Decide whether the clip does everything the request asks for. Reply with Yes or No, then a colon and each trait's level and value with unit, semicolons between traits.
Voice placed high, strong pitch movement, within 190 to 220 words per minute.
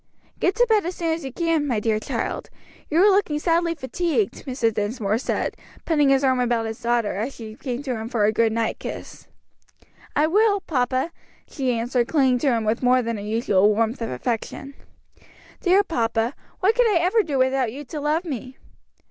Yes: very high, 260 Hz; wide, 6.1 semitones; average, 200 wpm